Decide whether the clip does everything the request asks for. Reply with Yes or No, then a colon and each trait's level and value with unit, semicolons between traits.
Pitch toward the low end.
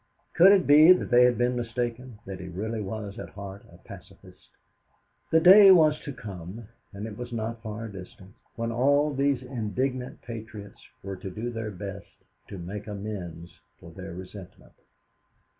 Yes: low, 110 Hz